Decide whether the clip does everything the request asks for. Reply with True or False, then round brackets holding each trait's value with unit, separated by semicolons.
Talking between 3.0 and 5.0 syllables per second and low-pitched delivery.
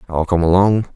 False (5.4 syllables/s; 90 Hz)